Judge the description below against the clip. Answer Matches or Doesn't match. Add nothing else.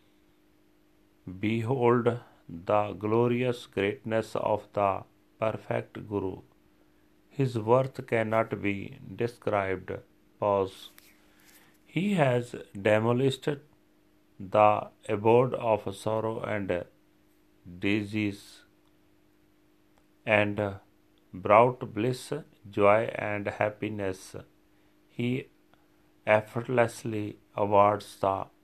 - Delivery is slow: Matches